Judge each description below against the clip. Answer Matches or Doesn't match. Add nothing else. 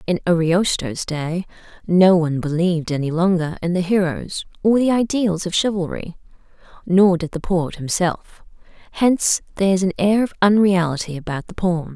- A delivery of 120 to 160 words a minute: Matches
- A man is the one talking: Doesn't match